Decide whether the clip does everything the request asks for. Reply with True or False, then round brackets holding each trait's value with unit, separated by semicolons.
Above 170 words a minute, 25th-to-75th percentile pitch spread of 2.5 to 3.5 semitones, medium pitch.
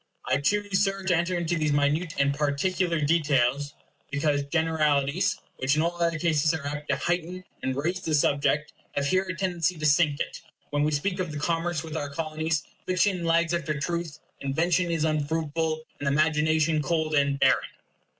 True (180 wpm; 2.9 semitones; 155 Hz)